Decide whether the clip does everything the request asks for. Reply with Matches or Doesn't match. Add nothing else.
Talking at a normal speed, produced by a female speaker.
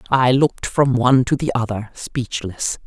Matches